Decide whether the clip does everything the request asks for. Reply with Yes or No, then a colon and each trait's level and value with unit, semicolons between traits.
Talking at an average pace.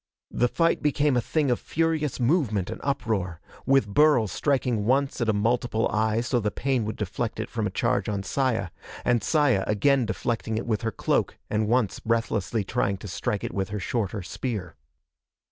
Yes: average, 185 wpm